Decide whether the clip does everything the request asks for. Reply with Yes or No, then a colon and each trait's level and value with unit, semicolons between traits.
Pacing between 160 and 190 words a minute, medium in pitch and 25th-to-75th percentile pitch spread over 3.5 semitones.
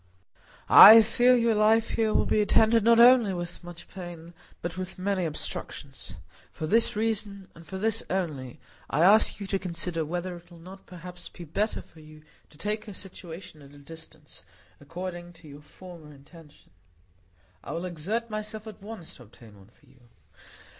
Yes: average, 170 wpm; medium, 180 Hz; average, 4.7 semitones